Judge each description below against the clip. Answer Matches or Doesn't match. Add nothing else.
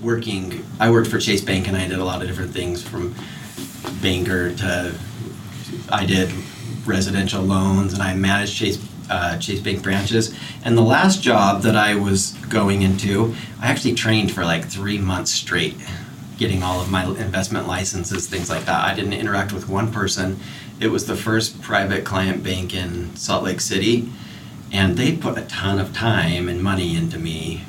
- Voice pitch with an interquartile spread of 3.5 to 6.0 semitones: Doesn't match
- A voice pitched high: Doesn't match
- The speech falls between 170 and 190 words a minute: Matches